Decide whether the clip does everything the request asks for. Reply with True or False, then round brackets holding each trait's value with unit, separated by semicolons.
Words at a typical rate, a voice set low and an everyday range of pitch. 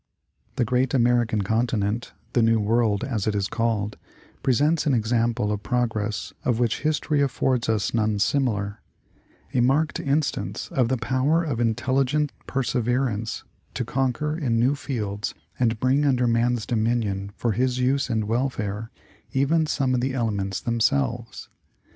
True (150 wpm; 120 Hz; 3.2 semitones)